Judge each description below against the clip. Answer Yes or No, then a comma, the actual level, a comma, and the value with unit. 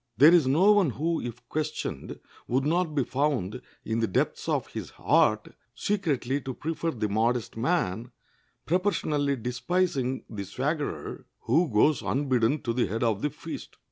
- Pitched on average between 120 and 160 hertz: Yes, low, 135 Hz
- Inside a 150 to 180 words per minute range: Yes, average, 155 wpm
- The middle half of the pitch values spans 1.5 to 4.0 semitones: No, average, 5.1 semitones